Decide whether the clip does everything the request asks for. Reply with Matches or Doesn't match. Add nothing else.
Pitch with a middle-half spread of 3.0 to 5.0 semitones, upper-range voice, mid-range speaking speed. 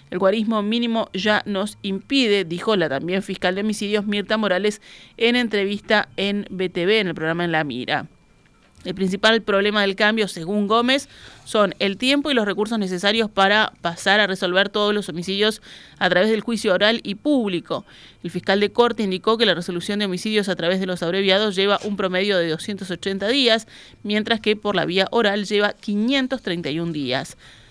Doesn't match